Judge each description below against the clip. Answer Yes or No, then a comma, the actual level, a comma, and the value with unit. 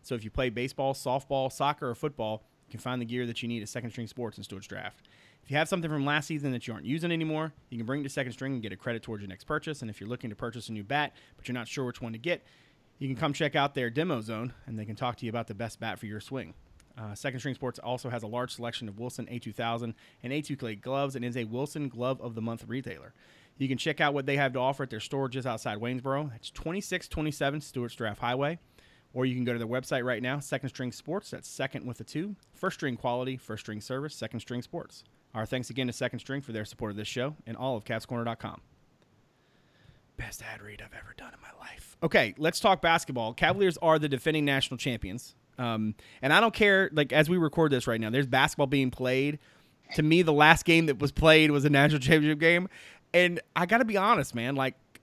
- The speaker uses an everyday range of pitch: Yes, average, 3.9 semitones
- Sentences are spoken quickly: Yes, fast, 255 wpm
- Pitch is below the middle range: Yes, low, 130 Hz